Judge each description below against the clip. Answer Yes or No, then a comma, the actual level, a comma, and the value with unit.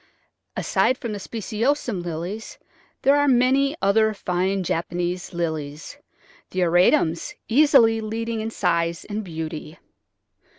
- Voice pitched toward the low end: No, high, 200 Hz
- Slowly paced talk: Yes, slow, 115 wpm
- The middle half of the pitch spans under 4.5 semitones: No, average, 5.0 semitones